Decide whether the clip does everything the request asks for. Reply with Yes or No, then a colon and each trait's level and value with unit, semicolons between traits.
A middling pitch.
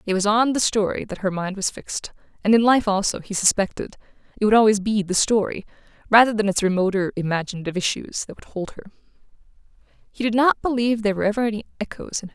No: high, 210 Hz